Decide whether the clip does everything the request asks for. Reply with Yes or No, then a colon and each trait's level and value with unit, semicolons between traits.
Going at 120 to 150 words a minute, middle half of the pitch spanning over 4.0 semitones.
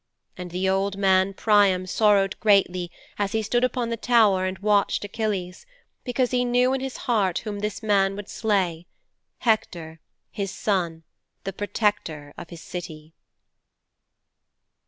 No: average, 140 wpm; average, 3.1 semitones